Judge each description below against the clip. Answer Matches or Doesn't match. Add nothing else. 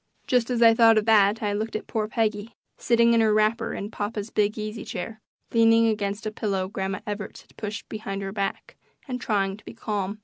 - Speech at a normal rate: Doesn't match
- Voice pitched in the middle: Doesn't match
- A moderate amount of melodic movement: Doesn't match